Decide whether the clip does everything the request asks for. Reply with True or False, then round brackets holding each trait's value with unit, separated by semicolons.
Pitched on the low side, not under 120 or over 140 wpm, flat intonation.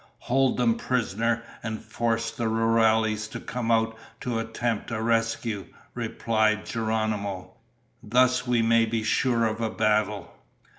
True (115 Hz; 135 wpm; 1.1 semitones)